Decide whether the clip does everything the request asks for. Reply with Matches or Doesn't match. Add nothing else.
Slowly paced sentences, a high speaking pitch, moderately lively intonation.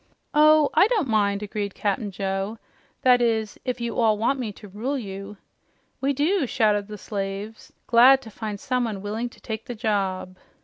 Doesn't match